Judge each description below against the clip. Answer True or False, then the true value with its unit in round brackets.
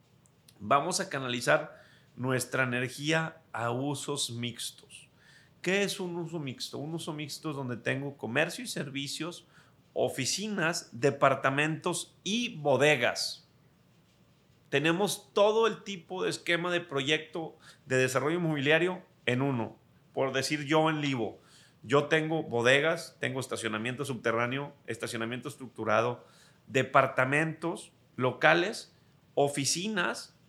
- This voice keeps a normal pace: False (110 wpm)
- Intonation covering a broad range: False (4.2 semitones)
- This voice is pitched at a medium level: True (145 Hz)